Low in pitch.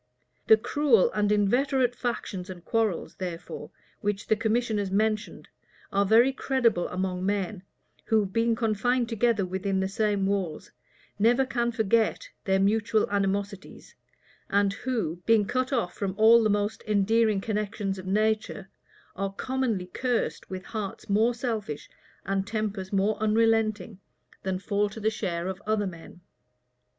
No: high, 210 Hz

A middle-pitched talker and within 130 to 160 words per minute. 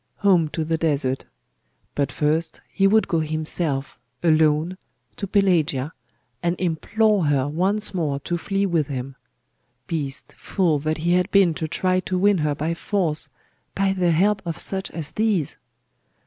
Yes: medium, 165 Hz; average, 155 wpm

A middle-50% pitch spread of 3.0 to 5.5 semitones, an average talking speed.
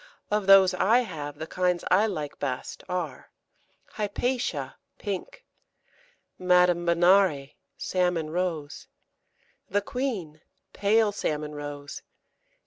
No: average, 4.7 semitones; slow, 100 wpm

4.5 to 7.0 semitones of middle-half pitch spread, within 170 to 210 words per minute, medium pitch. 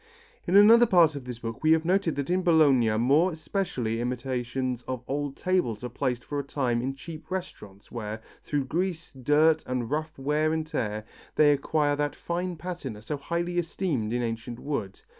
Yes: average, 5.1 semitones; average, 180 wpm; medium, 145 Hz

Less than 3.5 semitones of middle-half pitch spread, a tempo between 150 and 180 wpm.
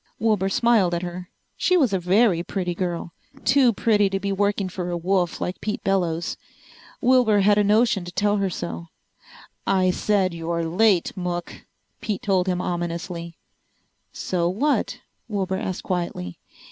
Yes: average, 2.9 semitones; average, 155 wpm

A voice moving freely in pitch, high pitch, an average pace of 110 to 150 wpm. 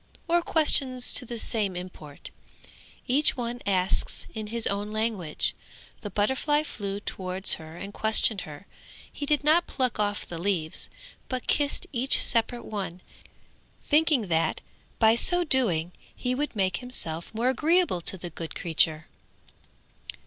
Yes: wide, 6.0 semitones; high, 215 Hz; average, 140 wpm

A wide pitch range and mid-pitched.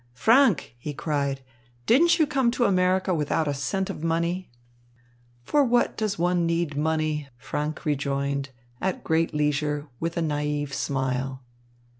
No: average, 4.3 semitones; medium, 155 Hz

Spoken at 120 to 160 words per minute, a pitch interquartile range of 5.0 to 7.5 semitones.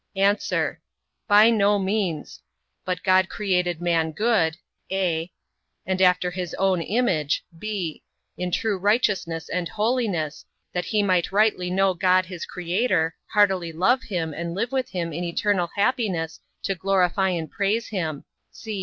No: average, 140 wpm; average, 3.2 semitones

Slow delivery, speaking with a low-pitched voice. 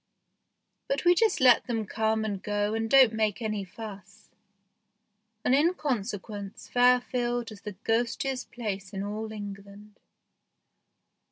No: slow, 125 wpm; high, 220 Hz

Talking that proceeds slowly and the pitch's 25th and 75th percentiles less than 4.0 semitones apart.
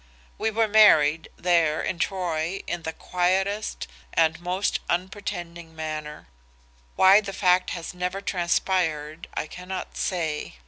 Yes: slow, 125 wpm; average, 2.9 semitones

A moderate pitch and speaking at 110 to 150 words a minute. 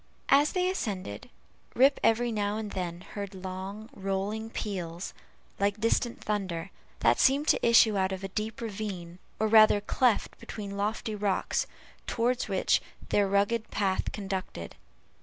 No: high, 205 Hz; average, 140 wpm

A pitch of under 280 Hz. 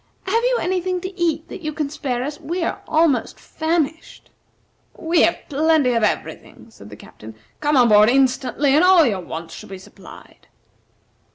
No: very high, 300 Hz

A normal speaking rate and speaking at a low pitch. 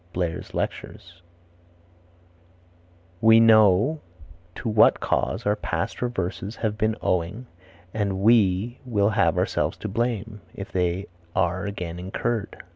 No: slow, 120 wpm; low, 105 Hz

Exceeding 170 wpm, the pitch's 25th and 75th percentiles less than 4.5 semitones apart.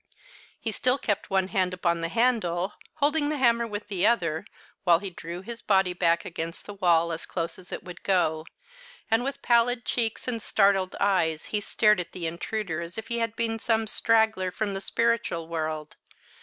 No: average, 190 wpm; average, 5.0 semitones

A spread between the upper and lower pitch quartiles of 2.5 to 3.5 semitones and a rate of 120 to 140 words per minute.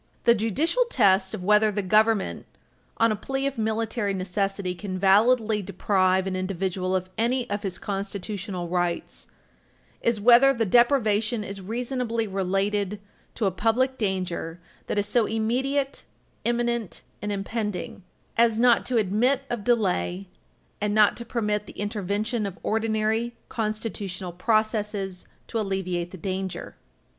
Yes: average, 3.1 semitones; slow, 135 wpm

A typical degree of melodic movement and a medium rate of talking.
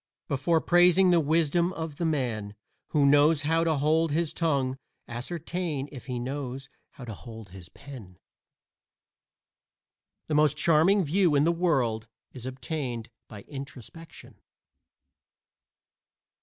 No: average, 4.4 semitones; slow, 125 wpm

